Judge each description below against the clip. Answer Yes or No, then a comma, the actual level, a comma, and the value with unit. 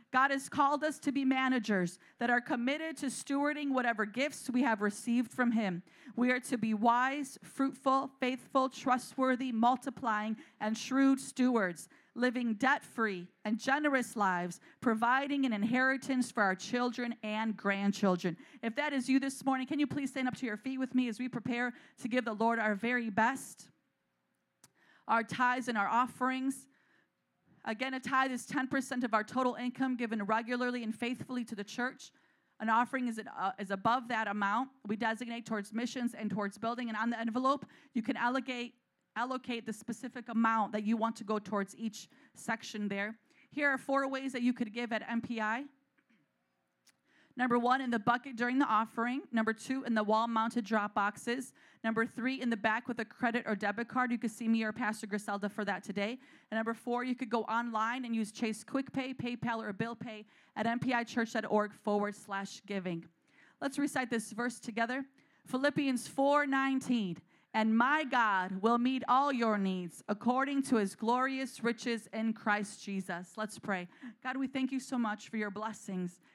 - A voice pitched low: No, high, 240 Hz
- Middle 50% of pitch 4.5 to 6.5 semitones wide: No, average, 3.0 semitones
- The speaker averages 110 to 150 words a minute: No, average, 180 wpm